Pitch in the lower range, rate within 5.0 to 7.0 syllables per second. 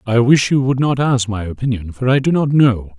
Yes: low, 125 Hz; 5.3 syllables/s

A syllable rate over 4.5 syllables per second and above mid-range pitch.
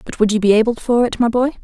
Yes: 6.7 syllables/s; high, 230 Hz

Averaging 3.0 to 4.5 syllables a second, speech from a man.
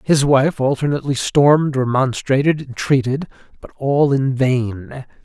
Yes: 4.4 syllables/s; male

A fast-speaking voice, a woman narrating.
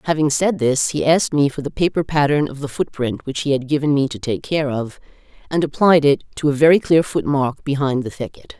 Yes: fast, 230 wpm; female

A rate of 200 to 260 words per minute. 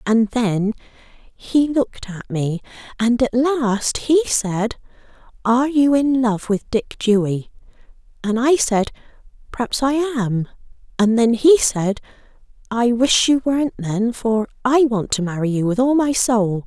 No: average, 155 wpm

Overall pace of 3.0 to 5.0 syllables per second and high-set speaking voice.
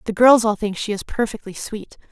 No: 5.4 syllables/s; high, 215 Hz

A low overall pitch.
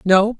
No: high, 205 Hz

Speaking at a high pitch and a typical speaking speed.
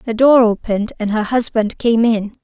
Yes: high, 225 Hz; average, 195 wpm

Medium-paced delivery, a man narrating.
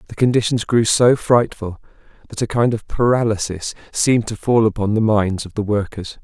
Yes: average, 185 wpm; male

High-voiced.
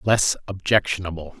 No: very low, 95 Hz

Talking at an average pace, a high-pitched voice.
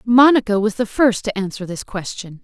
Yes: average, 195 wpm; high, 215 Hz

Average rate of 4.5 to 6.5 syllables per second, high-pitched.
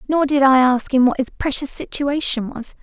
Yes: 5.2 syllables/s; very high, 270 Hz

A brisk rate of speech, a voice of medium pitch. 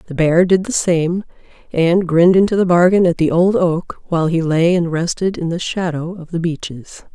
Yes: fast, 210 wpm; medium, 170 Hz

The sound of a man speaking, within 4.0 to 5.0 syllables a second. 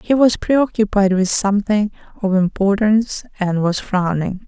No: female; 4.6 syllables/s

